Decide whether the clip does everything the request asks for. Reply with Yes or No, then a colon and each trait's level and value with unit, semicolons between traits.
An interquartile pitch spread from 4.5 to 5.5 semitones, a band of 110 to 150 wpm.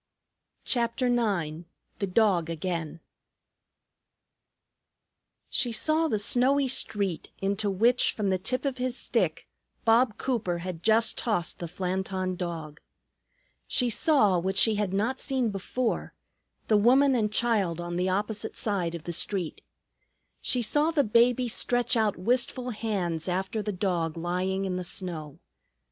Yes: average, 5.0 semitones; average, 140 wpm